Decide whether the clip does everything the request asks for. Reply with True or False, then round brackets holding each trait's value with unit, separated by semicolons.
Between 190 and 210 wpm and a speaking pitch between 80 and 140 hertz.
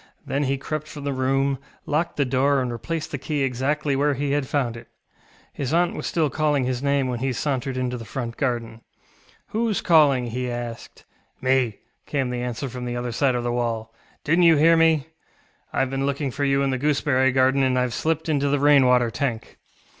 True (205 wpm; 135 Hz)